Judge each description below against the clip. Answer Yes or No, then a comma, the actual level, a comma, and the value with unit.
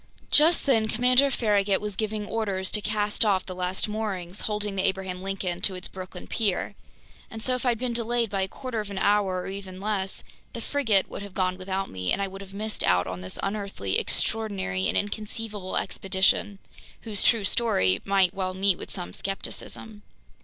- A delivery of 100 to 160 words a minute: No, average, 190 wpm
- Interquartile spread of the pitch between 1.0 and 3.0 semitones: Yes, narrow, 2.6 semitones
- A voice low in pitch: No, high, 200 Hz